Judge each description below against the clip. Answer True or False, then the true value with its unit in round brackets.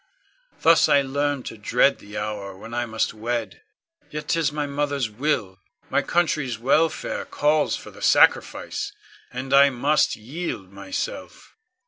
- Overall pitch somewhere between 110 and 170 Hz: True (135 Hz)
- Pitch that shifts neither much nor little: True (5.0 semitones)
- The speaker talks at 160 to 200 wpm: False (140 wpm)